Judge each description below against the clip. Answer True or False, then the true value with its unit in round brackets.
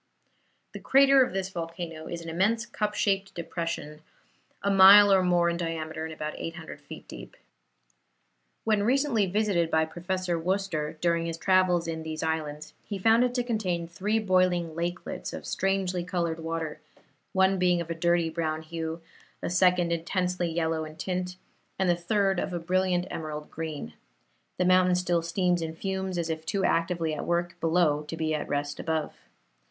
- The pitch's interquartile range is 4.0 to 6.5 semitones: False (2.7 semitones)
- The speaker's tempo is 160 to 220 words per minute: True (170 wpm)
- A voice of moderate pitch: True (175 Hz)